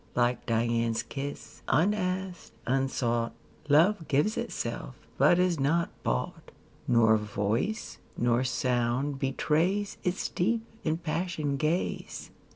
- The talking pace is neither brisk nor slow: No, slow, 105 wpm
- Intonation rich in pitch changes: Yes, wide, 6.7 semitones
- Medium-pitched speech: Yes, medium, 145 Hz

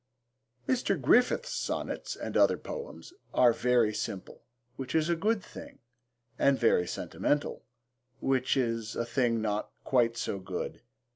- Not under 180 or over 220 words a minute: No, slow, 135 wpm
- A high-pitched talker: No, low, 125 Hz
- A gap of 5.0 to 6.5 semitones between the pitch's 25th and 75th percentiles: Yes, average, 5.3 semitones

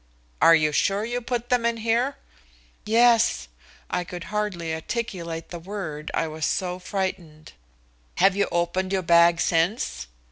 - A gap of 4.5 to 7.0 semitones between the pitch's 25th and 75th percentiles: Yes, average, 5.0 semitones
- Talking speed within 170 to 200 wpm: No, average, 145 wpm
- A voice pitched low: No, medium, 185 Hz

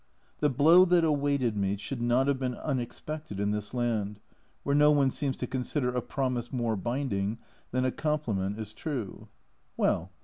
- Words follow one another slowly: No, average, 175 wpm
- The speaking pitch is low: Yes, low, 125 Hz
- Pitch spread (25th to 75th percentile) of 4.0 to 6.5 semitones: Yes, average, 4.7 semitones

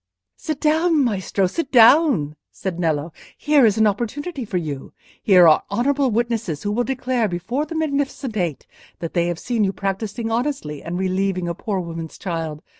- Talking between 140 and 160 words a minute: No, average, 175 wpm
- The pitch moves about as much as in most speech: No, wide, 7.2 semitones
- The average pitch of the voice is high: Yes, high, 210 Hz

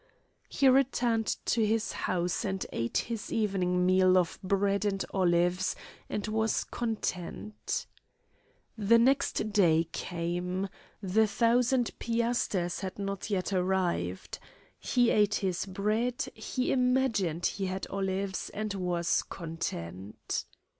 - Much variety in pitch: No, average, 3.7 semitones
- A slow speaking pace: Yes, slow, 115 wpm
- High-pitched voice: Yes, high, 195 Hz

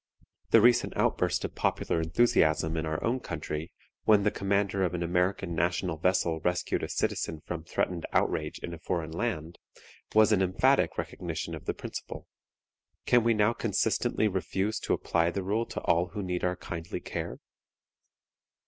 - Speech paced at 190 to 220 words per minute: No, average, 165 wpm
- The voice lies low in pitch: Yes, very low, 90 Hz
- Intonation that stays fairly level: No, average, 3.8 semitones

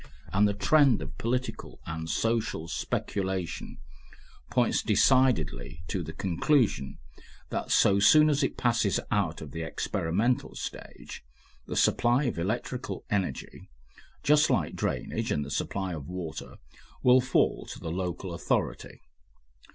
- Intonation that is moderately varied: No, wide, 7.1 semitones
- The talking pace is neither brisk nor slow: No, slow, 130 wpm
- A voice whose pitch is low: Yes, very low, 95 Hz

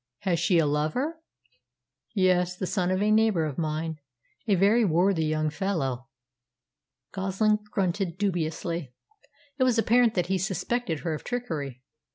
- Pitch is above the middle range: No, medium, 180 Hz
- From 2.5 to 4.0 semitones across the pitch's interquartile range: No, average, 4.7 semitones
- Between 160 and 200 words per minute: No, average, 145 wpm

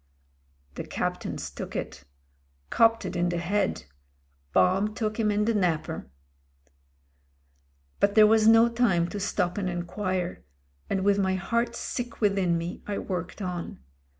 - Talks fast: No, average, 145 wpm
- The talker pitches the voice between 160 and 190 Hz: No, high, 200 Hz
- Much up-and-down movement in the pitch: No, average, 3.5 semitones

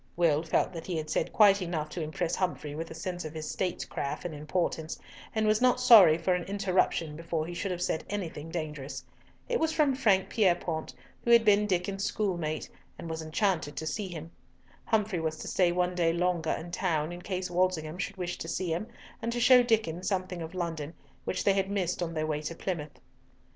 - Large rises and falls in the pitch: No, average, 3.4 semitones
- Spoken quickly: Yes, fast, 210 wpm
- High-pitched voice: No, medium, 175 Hz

